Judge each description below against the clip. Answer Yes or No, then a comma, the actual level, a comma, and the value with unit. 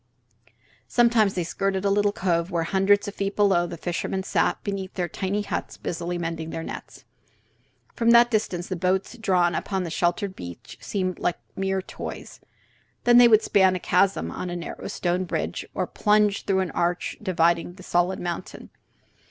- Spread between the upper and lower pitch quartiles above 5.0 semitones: No, narrow, 2.6 semitones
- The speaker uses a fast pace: No, average, 175 wpm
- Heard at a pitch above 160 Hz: Yes, high, 190 Hz